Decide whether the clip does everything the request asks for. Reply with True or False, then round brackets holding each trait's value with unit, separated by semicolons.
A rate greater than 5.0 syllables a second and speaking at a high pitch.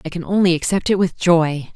False (5.5 syllables/s; 175 Hz)